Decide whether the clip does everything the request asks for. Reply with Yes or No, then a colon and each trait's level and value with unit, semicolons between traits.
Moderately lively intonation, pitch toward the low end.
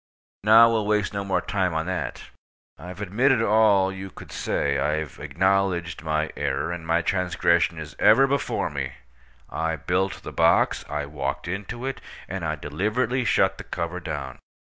Yes: average, 4.7 semitones; very low, 90 Hz